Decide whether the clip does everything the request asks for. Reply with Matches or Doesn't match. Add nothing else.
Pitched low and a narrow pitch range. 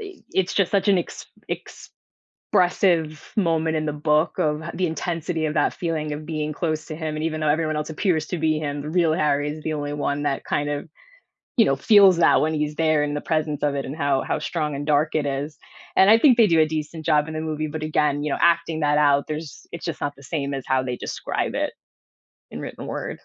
Doesn't match